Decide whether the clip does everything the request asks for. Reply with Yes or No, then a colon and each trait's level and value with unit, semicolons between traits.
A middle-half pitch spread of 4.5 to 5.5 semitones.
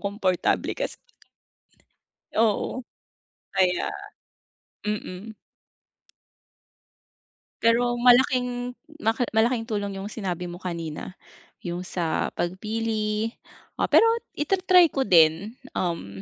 Yes: average, 4.8 semitones